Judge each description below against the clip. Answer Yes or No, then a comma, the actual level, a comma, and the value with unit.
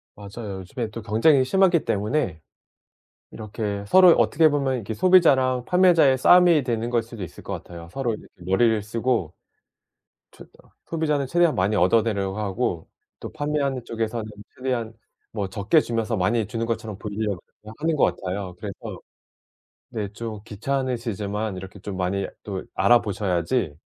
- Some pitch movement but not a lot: Yes, average, 4.6 semitones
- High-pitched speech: No, low, 115 Hz